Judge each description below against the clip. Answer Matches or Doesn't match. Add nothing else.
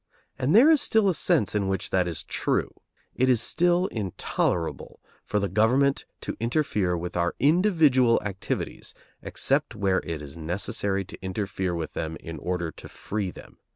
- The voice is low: Matches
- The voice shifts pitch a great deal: Matches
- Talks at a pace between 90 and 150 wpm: Doesn't match